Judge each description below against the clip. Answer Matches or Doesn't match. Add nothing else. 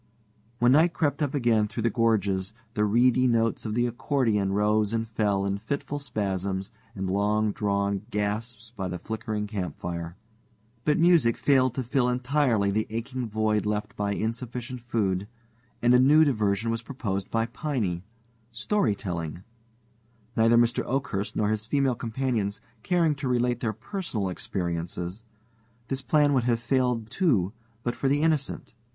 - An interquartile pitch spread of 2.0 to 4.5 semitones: Matches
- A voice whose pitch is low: Matches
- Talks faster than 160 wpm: Doesn't match